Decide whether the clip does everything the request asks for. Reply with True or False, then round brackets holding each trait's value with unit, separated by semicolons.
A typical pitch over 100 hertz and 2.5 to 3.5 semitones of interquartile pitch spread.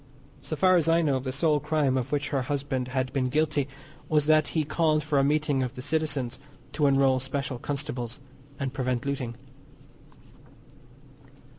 True (140 Hz; 2.8 semitones)